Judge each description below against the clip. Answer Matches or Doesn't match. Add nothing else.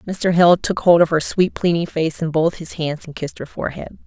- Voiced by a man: Doesn't match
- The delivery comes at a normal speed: Doesn't match